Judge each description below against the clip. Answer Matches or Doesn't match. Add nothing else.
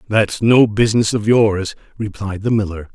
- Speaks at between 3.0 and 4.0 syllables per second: Doesn't match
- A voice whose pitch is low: Matches